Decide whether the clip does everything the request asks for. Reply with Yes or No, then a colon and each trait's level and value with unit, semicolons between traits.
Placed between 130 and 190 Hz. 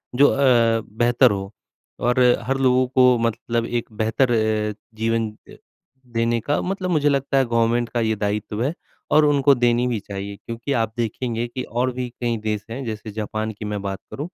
No: low, 120 Hz